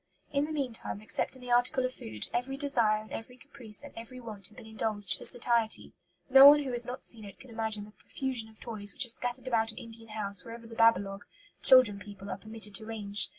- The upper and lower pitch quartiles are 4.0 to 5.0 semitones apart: No, average, 2.9 semitones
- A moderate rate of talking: No, fast, 230 wpm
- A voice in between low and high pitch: No, high, 225 Hz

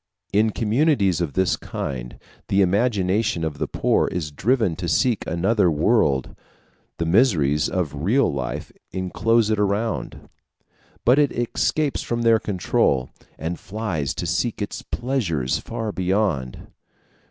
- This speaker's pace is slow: Yes, slow, 130 wpm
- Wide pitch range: Yes, wide, 5.9 semitones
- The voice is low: Yes, very low, 95 Hz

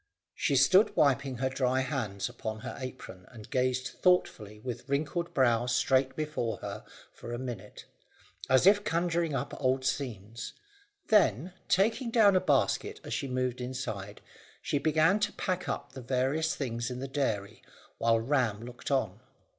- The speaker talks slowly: No, average, 155 wpm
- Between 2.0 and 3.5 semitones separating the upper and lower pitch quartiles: No, average, 4.6 semitones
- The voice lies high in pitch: No, low, 130 Hz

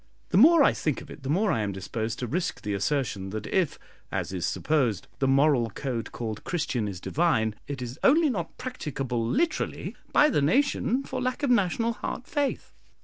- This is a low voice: No, medium, 145 Hz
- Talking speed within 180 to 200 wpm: Yes, average, 195 wpm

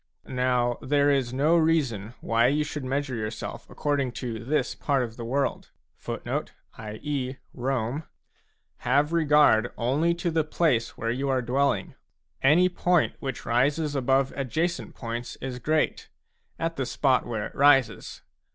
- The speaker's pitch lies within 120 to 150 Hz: Yes, low, 135 Hz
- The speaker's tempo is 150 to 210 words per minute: No, average, 140 wpm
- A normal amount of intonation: Yes, average, 3.6 semitones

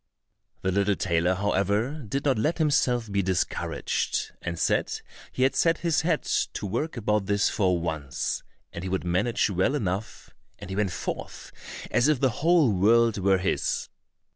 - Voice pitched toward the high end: No, low, 105 Hz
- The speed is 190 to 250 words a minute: No, average, 165 wpm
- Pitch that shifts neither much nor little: No, wide, 5.9 semitones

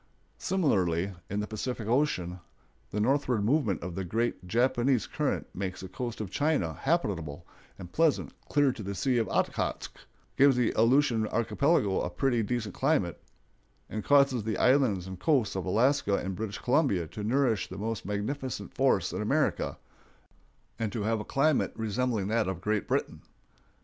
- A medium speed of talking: Yes, average, 160 wpm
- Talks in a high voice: No, low, 110 Hz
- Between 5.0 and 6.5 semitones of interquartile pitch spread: Yes, average, 5.3 semitones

